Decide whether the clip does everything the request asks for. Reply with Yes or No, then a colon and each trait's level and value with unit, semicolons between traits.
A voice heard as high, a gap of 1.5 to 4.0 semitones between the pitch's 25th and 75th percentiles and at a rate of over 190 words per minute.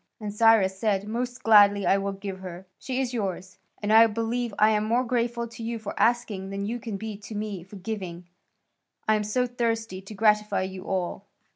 Yes: high, 210 Hz; average, 2.8 semitones; fast, 205 wpm